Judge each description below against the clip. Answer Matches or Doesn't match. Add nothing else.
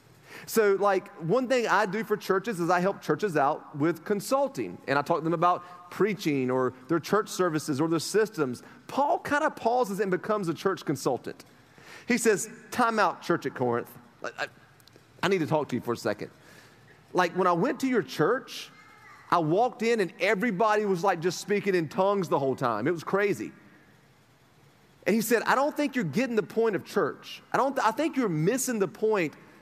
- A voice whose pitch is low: Doesn't match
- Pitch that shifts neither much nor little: Doesn't match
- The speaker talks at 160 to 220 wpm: Matches